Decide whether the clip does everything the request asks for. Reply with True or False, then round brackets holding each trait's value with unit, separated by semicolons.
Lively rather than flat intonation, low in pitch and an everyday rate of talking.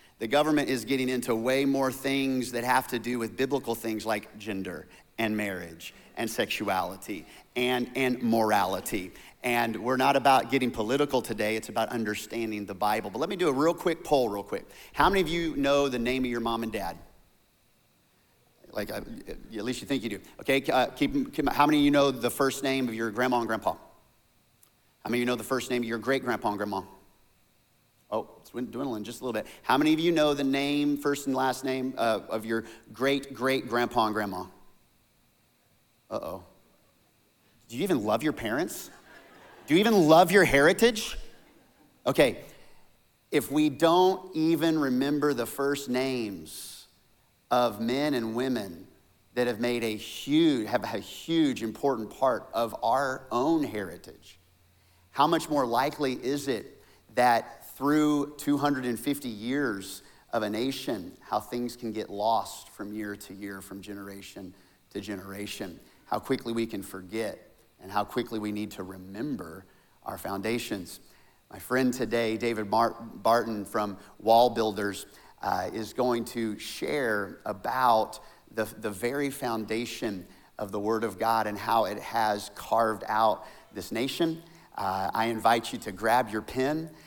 False (4.1 semitones; 120 Hz; 165 wpm)